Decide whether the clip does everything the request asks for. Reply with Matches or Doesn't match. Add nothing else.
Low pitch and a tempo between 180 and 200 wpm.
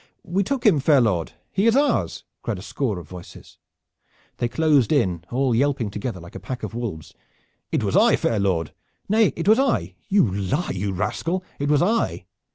Matches